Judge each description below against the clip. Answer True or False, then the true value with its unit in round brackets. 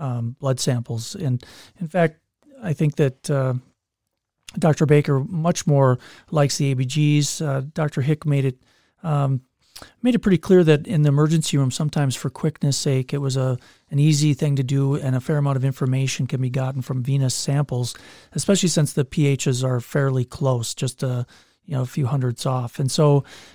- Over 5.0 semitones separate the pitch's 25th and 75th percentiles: False (2.7 semitones)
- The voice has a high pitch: False (140 Hz)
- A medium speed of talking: True (185 wpm)